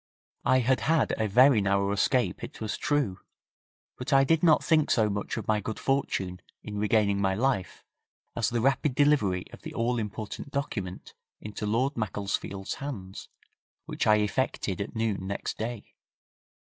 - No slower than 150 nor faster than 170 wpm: Yes, average, 160 wpm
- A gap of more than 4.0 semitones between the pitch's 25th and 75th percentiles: Yes, average, 4.7 semitones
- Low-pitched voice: Yes, low, 110 Hz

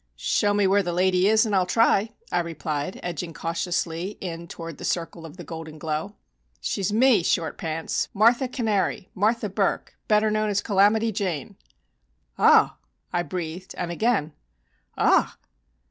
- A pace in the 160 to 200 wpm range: No, average, 145 wpm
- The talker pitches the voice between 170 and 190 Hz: Yes, medium, 185 Hz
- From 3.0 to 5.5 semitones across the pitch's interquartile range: Yes, average, 4.1 semitones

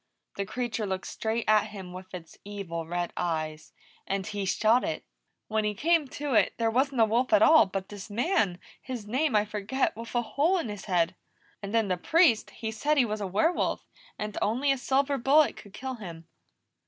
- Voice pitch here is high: Yes, high, 215 Hz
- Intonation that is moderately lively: Yes, average, 5.0 semitones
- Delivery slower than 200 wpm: No, fast, 205 wpm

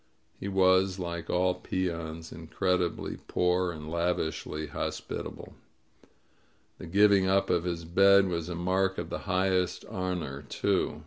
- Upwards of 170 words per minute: No, slow, 135 wpm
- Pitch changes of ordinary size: No, narrow, 2.0 semitones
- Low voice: Yes, very low, 90 Hz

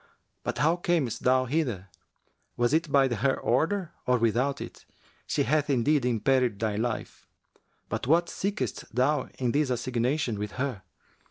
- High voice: No, low, 130 Hz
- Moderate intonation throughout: Yes, average, 4.1 semitones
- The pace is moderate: Yes, average, 150 wpm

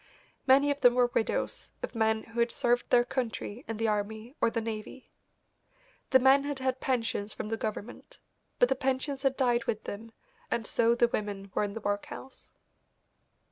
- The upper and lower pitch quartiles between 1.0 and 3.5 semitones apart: Yes, average, 3.0 semitones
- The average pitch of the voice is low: No, high, 235 Hz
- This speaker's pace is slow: No, average, 180 wpm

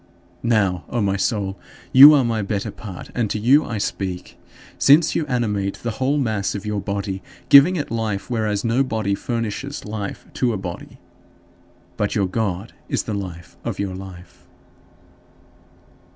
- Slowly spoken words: No, average, 160 wpm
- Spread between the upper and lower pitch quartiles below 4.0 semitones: Yes, average, 3.5 semitones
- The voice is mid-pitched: No, low, 105 Hz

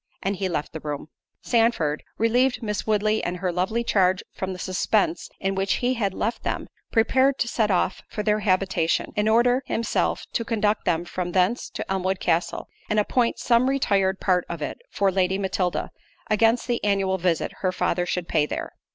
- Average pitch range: Yes, average, 3.7 semitones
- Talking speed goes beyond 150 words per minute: Yes, average, 190 wpm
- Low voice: No, high, 195 Hz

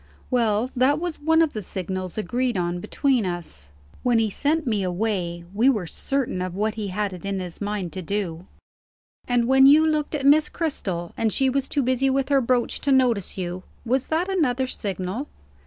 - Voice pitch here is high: Yes, high, 230 Hz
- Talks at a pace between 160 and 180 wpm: No, average, 195 wpm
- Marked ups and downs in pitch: Yes, wide, 6.4 semitones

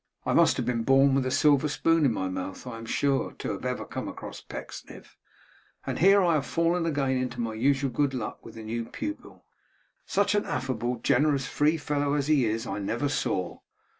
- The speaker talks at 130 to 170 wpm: No, fast, 205 wpm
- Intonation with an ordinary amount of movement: Yes, average, 4.2 semitones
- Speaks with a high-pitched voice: No, low, 135 Hz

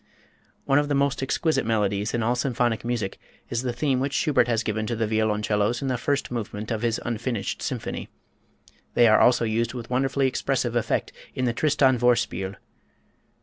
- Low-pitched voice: Yes, low, 120 Hz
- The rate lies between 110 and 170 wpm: No, average, 180 wpm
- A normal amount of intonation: Yes, average, 3.0 semitones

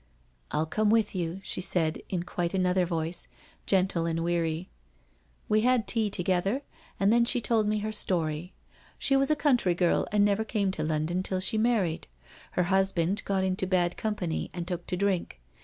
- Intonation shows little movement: No, average, 3.6 semitones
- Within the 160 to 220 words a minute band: Yes, average, 190 wpm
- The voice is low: No, medium, 185 Hz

